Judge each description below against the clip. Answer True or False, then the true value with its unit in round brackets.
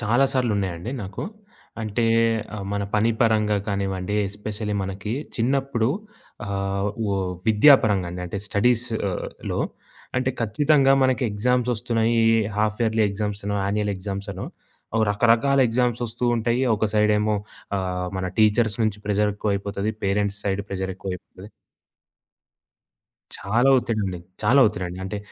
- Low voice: True (105 Hz)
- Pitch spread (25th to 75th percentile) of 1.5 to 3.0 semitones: True (2.7 semitones)